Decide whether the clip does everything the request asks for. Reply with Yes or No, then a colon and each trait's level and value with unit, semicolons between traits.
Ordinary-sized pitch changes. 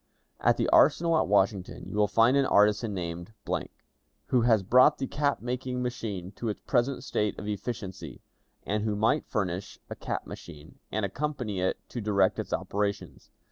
Yes: average, 4.2 semitones